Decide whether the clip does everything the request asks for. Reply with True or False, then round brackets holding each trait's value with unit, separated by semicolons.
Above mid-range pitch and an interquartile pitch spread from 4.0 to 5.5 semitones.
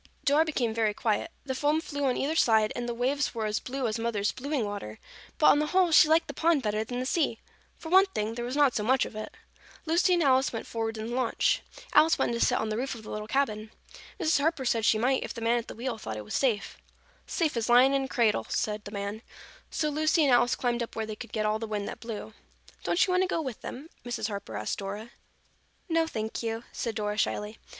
True (240 Hz; 4.8 semitones)